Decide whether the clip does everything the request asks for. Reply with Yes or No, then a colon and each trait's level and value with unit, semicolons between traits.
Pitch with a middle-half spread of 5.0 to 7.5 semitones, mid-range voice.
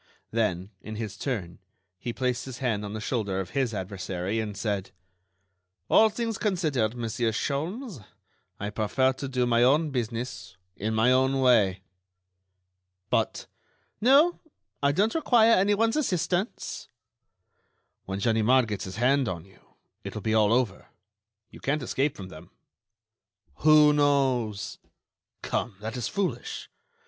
No: wide, 5.6 semitones; low, 120 Hz